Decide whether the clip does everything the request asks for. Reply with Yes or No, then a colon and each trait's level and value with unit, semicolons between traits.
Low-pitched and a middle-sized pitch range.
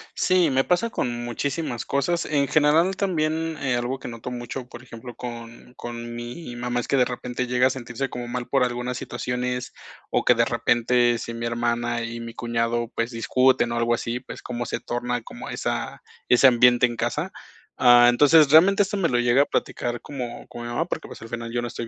No: low, 120 Hz; narrow, 2.1 semitones